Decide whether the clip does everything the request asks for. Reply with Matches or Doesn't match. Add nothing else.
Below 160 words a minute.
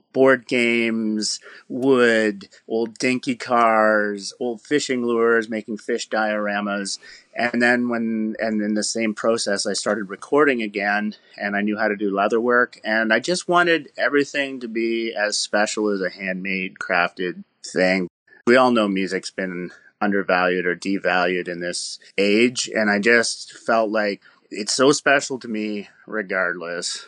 Matches